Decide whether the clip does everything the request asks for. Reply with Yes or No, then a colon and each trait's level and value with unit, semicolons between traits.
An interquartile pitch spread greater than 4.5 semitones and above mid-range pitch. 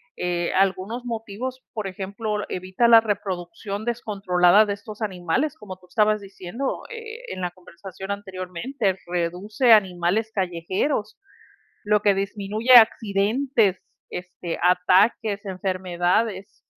No: average, 3.2 semitones; high, 200 Hz